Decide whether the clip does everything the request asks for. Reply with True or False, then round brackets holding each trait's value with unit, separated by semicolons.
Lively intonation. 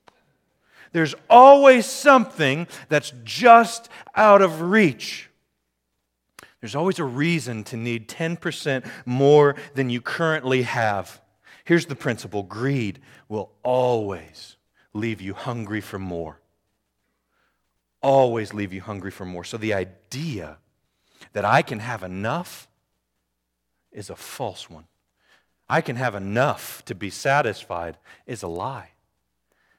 True (7.6 semitones)